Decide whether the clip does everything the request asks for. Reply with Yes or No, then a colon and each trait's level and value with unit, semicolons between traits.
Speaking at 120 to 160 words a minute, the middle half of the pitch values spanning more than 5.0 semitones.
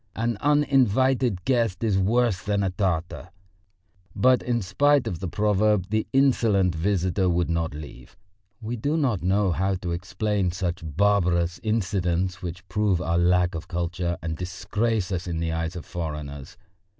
No: average, 155 wpm; average, 3.8 semitones